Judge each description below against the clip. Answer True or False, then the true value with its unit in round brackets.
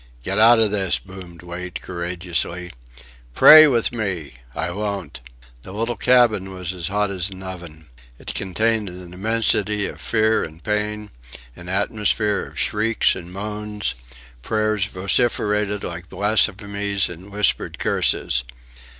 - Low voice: True (100 Hz)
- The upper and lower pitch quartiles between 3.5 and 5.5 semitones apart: False (3.0 semitones)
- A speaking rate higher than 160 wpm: False (140 wpm)